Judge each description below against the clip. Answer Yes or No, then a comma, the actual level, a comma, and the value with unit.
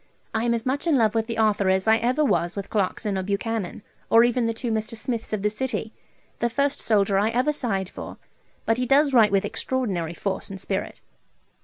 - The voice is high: Yes, high, 225 Hz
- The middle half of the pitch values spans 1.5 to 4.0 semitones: Yes, average, 3.4 semitones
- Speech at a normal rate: No, fast, 215 wpm